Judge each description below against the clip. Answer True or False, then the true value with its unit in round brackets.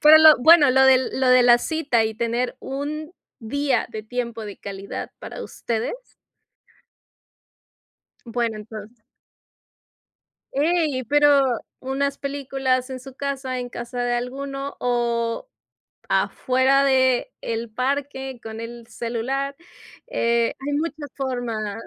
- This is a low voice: False (255 Hz)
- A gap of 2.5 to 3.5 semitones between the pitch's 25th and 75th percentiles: True (2.9 semitones)